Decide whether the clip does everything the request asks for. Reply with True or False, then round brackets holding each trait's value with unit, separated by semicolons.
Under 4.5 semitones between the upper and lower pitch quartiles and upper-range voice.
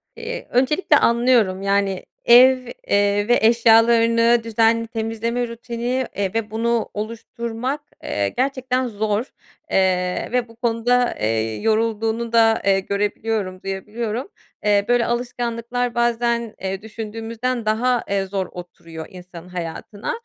True (2.9 semitones; 225 Hz)